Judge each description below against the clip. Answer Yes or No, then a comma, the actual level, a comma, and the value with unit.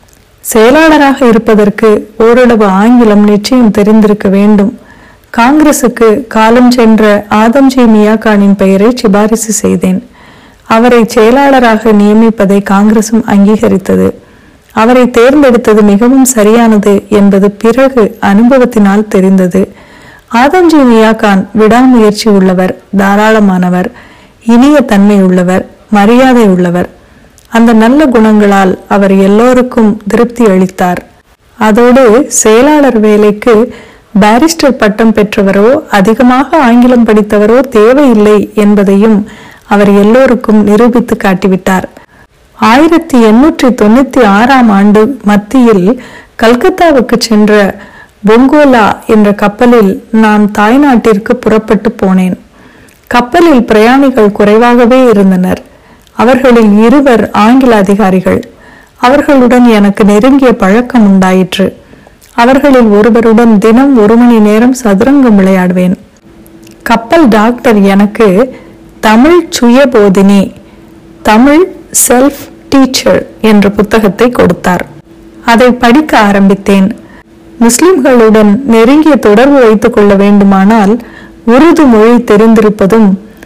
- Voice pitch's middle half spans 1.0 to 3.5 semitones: Yes, average, 3.0 semitones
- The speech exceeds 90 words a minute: No, average, 85 wpm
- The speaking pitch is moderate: No, high, 225 Hz